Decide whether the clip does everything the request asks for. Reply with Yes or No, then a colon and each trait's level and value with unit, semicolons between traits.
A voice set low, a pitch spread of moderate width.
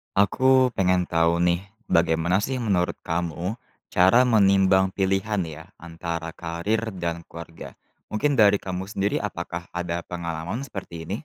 Yes: very low, 90 Hz; average, 3.3 semitones